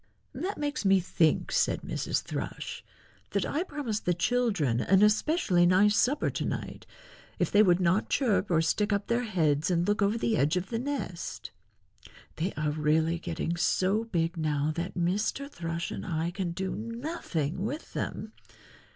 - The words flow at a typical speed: Yes, average, 170 wpm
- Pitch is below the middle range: No, medium, 185 Hz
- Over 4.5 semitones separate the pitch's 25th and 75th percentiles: Yes, average, 5.0 semitones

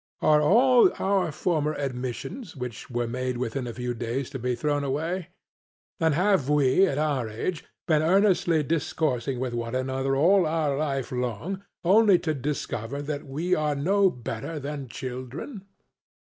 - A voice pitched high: No, medium, 145 Hz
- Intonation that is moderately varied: Yes, average, 4.8 semitones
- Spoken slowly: No, average, 155 wpm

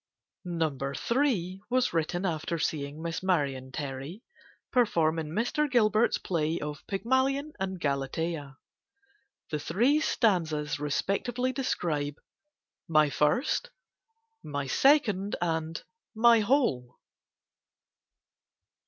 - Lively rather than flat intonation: Yes, wide, 7.9 semitones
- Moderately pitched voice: Yes, medium, 170 Hz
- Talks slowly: Yes, slow, 95 wpm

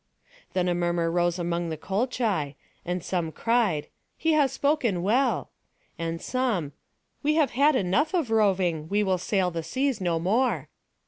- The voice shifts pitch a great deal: Yes, wide, 6.6 semitones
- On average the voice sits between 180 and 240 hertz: Yes, high, 190 Hz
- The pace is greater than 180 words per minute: No, average, 155 wpm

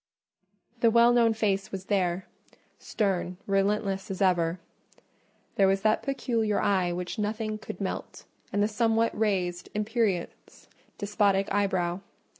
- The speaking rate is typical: No, slow, 120 wpm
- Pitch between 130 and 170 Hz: No, high, 200 Hz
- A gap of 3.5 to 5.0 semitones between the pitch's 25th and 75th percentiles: No, narrow, 2.6 semitones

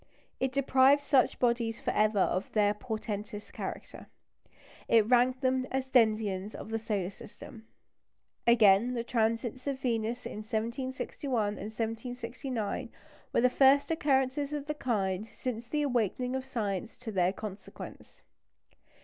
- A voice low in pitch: No, high, 235 Hz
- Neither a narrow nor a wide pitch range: Yes, average, 3.4 semitones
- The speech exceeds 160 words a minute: No, slow, 135 wpm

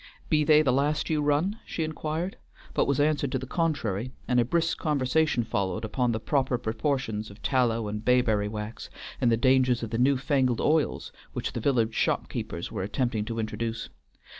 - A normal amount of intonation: Yes, average, 4.6 semitones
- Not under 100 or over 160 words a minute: No, average, 190 wpm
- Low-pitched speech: Yes, low, 125 Hz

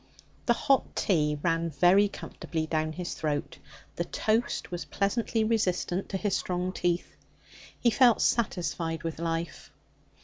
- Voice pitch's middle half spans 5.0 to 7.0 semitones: No, average, 4.3 semitones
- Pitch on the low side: No, medium, 180 Hz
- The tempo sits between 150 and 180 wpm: No, slow, 135 wpm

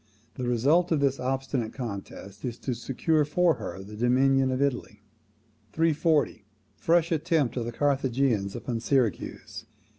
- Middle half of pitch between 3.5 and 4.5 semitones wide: Yes, average, 4.0 semitones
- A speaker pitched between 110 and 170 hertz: Yes, low, 135 Hz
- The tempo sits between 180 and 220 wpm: No, average, 140 wpm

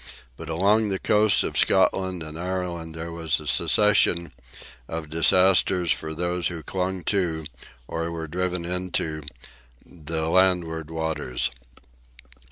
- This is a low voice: Yes, very low, 85 Hz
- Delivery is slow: Yes, slow, 125 wpm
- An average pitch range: No, narrow, 2.2 semitones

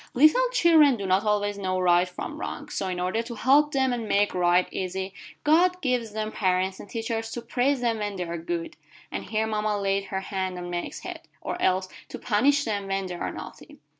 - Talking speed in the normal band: No, fast, 215 wpm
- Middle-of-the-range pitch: No, high, 205 Hz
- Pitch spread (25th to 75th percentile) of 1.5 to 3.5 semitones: No, average, 4.6 semitones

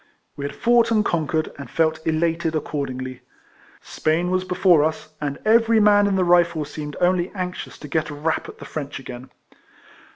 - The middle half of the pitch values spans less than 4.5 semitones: Yes, average, 3.8 semitones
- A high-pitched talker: No, medium, 160 Hz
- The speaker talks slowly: No, average, 175 wpm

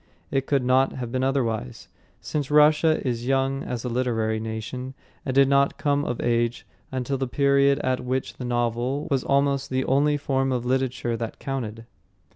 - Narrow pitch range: Yes, narrow, 2.3 semitones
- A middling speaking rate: Yes, average, 175 wpm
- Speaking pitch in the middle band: No, low, 130 Hz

